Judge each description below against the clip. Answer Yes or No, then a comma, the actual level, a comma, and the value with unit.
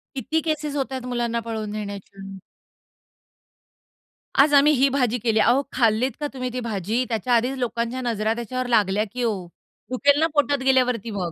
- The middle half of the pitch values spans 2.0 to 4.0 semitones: Yes, average, 3.5 semitones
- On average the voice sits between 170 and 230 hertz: No, high, 245 Hz